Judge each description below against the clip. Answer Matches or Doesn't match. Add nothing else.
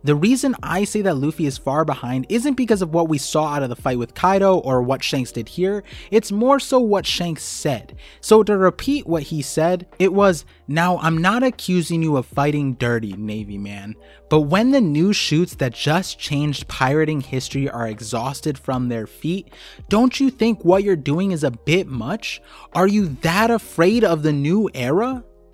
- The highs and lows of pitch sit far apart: Matches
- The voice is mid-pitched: Matches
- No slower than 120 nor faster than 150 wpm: Doesn't match